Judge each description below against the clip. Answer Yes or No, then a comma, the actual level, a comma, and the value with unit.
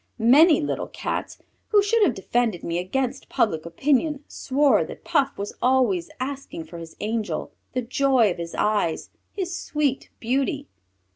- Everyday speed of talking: Yes, average, 150 wpm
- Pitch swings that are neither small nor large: No, wide, 5.9 semitones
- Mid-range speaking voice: No, very high, 255 Hz